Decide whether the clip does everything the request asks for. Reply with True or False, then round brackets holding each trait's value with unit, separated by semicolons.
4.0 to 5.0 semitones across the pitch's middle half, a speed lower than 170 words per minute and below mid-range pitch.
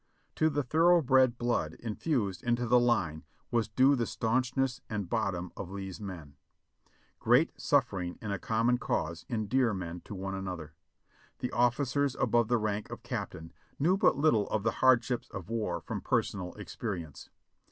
True (4.5 semitones; 160 wpm; 115 Hz)